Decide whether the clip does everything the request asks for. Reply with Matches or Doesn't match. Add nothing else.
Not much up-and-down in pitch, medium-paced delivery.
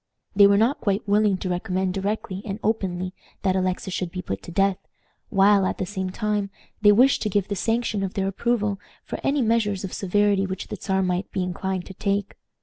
Doesn't match